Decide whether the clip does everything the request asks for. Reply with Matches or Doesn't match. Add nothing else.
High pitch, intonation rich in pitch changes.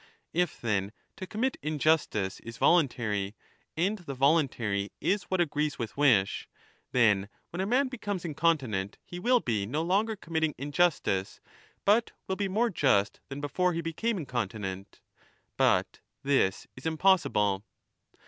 Doesn't match